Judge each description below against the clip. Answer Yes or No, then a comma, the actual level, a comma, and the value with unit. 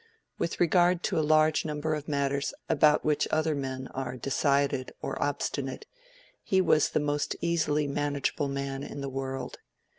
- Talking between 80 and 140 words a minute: No, average, 155 wpm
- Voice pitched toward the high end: No, medium, 145 Hz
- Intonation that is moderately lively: No, narrow, 2.1 semitones